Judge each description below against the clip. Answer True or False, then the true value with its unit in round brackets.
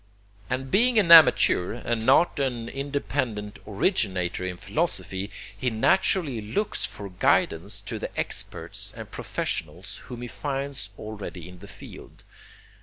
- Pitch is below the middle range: True (115 Hz)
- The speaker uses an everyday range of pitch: False (5.9 semitones)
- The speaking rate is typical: False (130 wpm)